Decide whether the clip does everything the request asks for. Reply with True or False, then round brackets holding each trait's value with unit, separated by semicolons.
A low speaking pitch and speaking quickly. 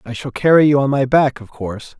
True (130 Hz; 270 wpm)